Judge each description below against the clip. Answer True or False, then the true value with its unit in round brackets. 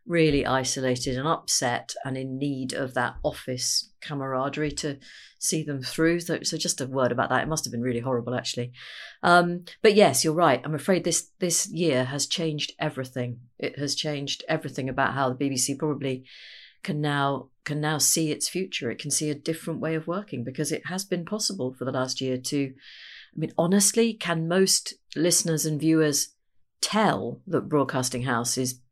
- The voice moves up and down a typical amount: True (4.0 semitones)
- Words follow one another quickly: False (185 wpm)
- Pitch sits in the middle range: True (145 Hz)